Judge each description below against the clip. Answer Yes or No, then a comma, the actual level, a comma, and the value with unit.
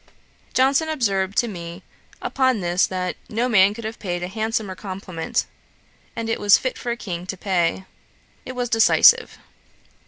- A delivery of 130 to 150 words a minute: No, average, 160 wpm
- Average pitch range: Yes, average, 4.3 semitones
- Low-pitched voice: No, high, 205 Hz